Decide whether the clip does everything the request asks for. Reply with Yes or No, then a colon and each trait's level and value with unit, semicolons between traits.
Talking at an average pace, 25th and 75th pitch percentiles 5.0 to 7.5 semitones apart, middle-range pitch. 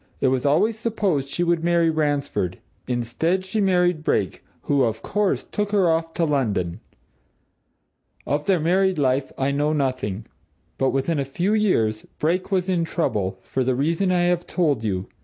Yes: average, 170 wpm; wide, 5.4 semitones; medium, 155 Hz